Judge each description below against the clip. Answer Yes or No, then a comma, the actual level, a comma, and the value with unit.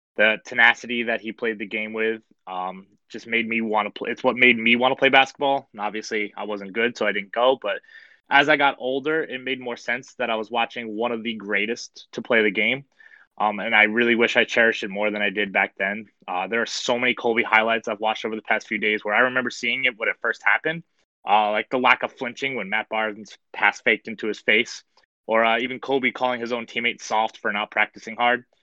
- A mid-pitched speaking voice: No, low, 115 Hz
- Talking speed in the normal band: No, fast, 245 wpm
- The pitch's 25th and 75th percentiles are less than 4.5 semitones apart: Yes, narrow, 2.5 semitones